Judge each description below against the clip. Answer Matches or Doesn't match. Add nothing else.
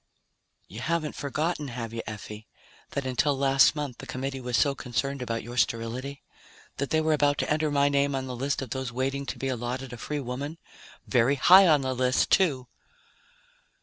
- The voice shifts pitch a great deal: Doesn't match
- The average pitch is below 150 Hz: Matches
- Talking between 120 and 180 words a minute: Doesn't match